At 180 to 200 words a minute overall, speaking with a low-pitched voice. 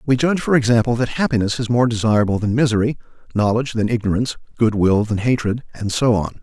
Yes: average, 185 wpm; low, 115 Hz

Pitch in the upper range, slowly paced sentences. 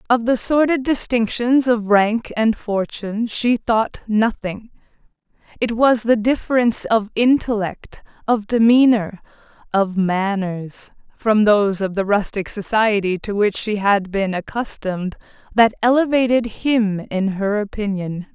Yes: high, 215 Hz; slow, 130 wpm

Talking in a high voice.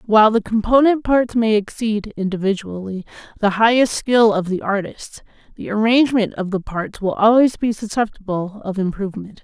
Yes: high, 210 Hz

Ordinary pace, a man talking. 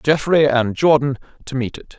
Yes: average, 180 wpm; male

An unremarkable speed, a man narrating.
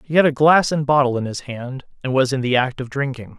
No: fast, 285 wpm; male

